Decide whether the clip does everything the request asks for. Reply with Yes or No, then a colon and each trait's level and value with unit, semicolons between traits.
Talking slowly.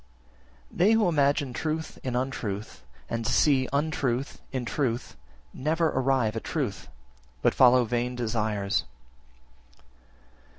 Yes: slow, 115 wpm